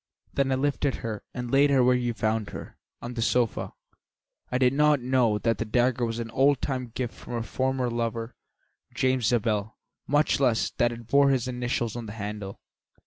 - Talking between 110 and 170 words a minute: No, average, 195 wpm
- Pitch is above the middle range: No, low, 120 Hz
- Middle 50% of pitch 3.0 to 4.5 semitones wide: No, narrow, 2.5 semitones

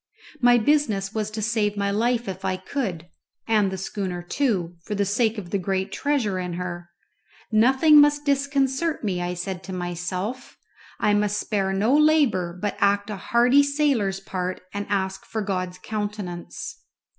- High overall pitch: Yes, high, 205 Hz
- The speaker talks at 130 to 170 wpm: Yes, average, 165 wpm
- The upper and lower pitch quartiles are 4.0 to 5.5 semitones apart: Yes, average, 4.4 semitones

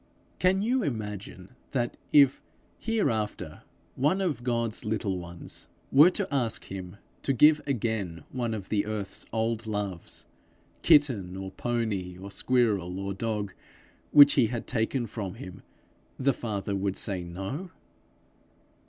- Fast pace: No, slow, 135 wpm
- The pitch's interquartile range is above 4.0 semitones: Yes, average, 5.2 semitones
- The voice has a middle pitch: No, low, 110 Hz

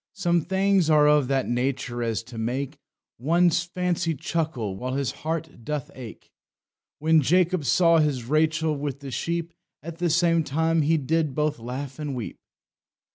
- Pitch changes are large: No, average, 4.1 semitones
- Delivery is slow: No, average, 160 wpm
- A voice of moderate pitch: Yes, medium, 150 Hz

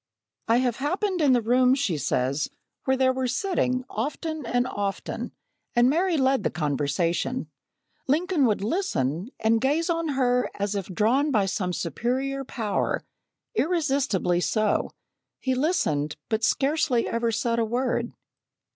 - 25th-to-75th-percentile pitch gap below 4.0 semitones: No, average, 5.2 semitones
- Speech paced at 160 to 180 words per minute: No, average, 140 wpm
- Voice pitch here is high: Yes, high, 245 Hz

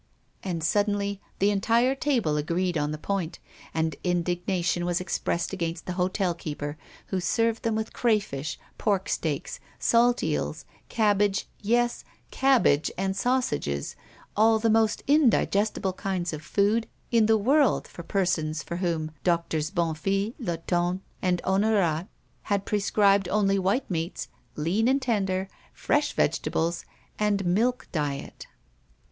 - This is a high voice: Yes, high, 195 Hz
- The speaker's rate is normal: No, slow, 130 wpm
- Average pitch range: Yes, average, 4.2 semitones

